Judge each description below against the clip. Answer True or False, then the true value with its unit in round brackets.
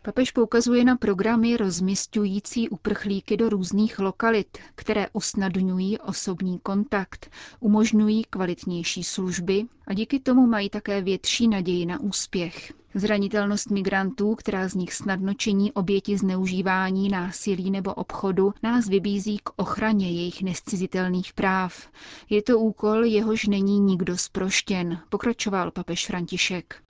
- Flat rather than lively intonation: True (2.2 semitones)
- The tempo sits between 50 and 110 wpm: False (120 wpm)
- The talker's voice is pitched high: True (200 Hz)